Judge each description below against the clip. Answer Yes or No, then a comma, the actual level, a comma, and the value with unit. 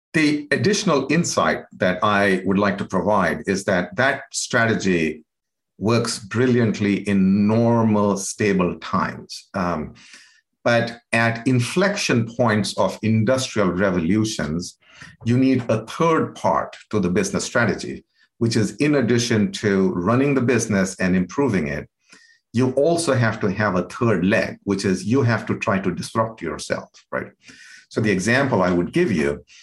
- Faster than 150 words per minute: No, average, 145 wpm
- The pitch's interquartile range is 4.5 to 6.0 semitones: Yes, average, 5.1 semitones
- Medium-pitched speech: No, low, 115 Hz